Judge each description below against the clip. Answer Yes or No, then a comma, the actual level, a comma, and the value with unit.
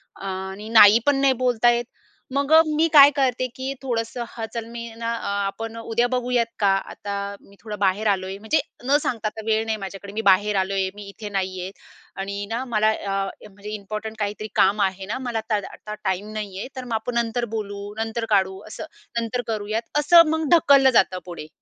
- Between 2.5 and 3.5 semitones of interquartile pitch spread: Yes, average, 3.2 semitones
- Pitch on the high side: Yes, high, 220 Hz